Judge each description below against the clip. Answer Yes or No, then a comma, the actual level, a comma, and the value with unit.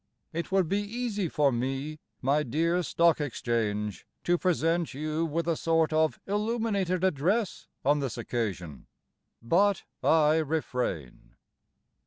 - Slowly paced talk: Yes, slow, 125 wpm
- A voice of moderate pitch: Yes, medium, 160 Hz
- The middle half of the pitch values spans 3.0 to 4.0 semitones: No, average, 5.0 semitones